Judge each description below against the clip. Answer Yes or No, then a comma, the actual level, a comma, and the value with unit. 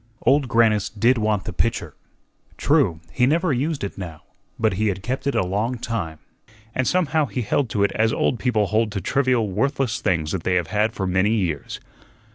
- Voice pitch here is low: Yes, low, 110 Hz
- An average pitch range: Yes, average, 4.8 semitones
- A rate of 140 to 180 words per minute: No, average, 200 wpm